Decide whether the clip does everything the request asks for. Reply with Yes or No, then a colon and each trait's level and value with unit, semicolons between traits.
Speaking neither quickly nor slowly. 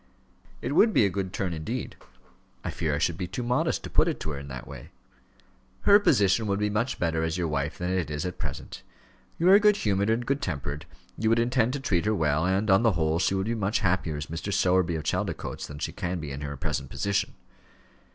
No: fast, 240 wpm